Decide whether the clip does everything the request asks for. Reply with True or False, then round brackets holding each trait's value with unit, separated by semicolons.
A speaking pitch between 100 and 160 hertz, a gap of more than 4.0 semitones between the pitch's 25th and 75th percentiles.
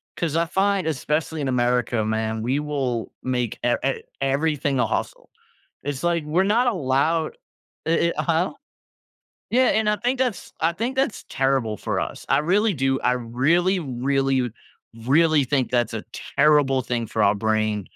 True (140 Hz; 5.2 semitones)